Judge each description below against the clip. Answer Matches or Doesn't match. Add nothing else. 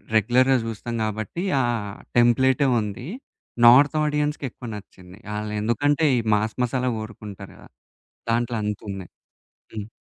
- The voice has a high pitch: Doesn't match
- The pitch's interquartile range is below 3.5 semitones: Doesn't match